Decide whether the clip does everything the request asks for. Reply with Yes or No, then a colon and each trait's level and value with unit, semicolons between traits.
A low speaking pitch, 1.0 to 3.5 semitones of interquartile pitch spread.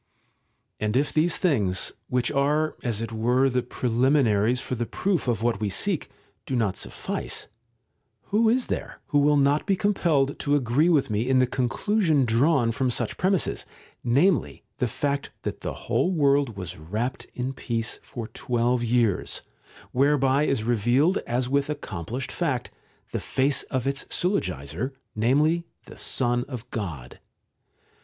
No: low, 130 Hz; average, 4.1 semitones